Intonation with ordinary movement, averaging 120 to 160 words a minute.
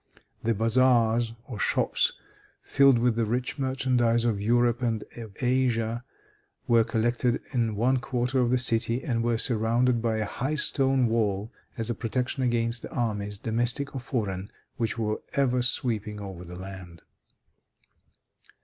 No: narrow, 2.1 semitones; average, 150 wpm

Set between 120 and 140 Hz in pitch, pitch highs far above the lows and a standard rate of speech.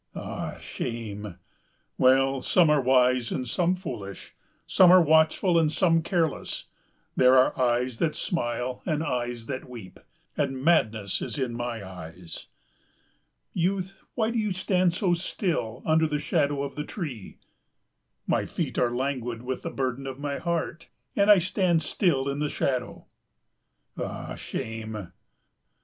Yes: low, 135 Hz; wide, 5.7 semitones; average, 145 wpm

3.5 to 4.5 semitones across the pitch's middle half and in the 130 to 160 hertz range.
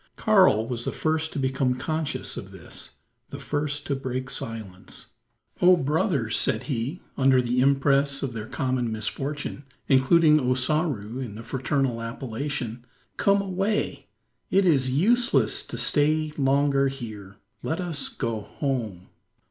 Yes: average, 4.1 semitones; low, 135 Hz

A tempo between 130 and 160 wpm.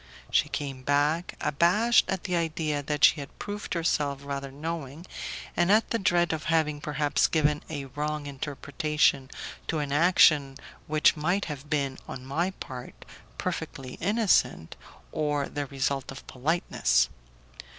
Yes: average, 140 wpm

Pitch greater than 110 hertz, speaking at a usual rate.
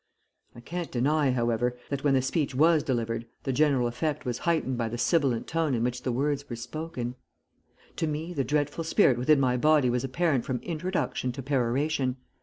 Yes: low, 135 Hz; average, 190 wpm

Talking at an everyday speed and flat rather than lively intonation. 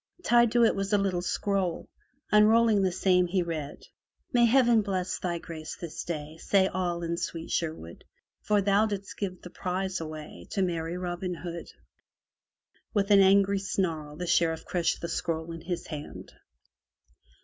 No: average, 160 wpm; average, 3.0 semitones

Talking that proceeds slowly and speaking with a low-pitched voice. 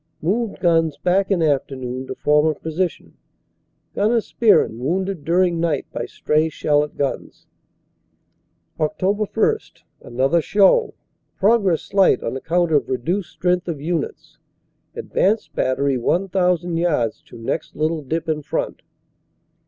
No: slow, 125 wpm; medium, 165 Hz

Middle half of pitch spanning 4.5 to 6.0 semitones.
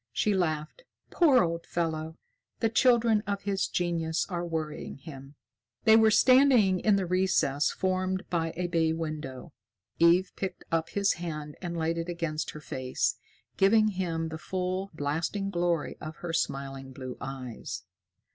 No: average, 3.5 semitones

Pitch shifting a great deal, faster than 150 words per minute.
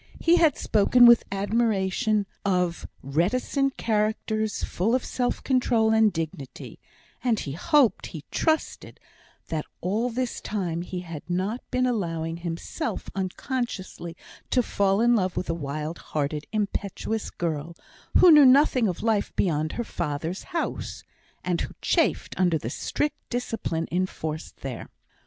No: wide, 6.1 semitones; average, 140 wpm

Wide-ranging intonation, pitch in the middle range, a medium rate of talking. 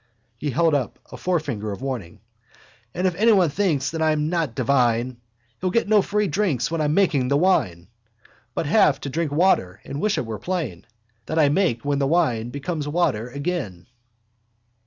Yes: wide, 6.0 semitones; medium, 150 Hz; average, 180 wpm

